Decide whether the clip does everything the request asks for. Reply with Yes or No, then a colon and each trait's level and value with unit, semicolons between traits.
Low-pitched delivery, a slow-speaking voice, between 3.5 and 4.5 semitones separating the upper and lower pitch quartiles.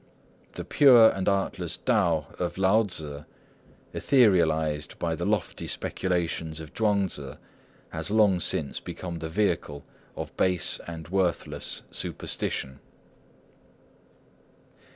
Yes: very low, 85 Hz; slow, 110 wpm; average, 3.8 semitones